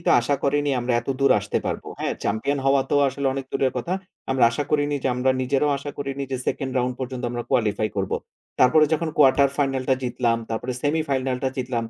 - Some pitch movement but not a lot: No, narrow, 2.2 semitones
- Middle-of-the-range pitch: No, low, 130 Hz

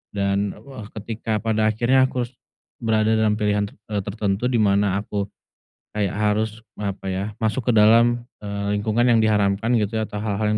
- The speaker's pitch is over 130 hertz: No, low, 105 Hz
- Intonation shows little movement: Yes, narrow, 1.8 semitones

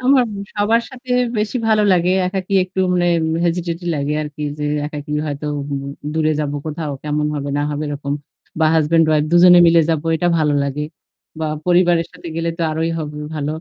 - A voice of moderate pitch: Yes, medium, 165 Hz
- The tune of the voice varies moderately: Yes, average, 3.1 semitones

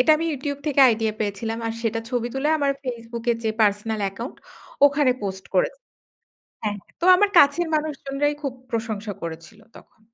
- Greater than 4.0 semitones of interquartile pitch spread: Yes, average, 4.7 semitones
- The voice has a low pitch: No, high, 235 Hz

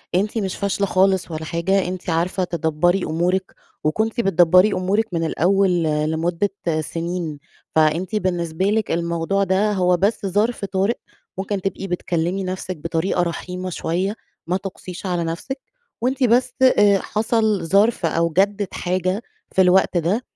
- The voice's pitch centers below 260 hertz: Yes, medium, 185 Hz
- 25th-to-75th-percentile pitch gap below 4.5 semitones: Yes, average, 2.7 semitones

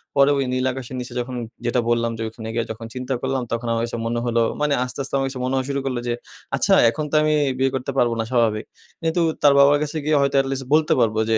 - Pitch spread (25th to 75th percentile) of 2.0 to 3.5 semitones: Yes, average, 2.8 semitones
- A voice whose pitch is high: No, low, 130 Hz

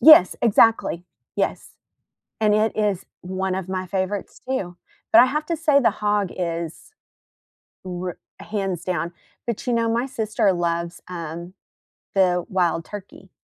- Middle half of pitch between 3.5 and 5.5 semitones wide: Yes, average, 3.8 semitones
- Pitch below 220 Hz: Yes, high, 190 Hz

